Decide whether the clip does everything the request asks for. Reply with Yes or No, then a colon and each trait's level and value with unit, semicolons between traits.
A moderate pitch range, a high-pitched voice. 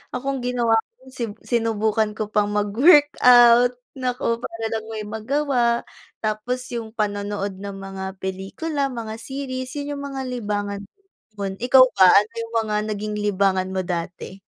Yes: average, 3.6 semitones; high, 220 Hz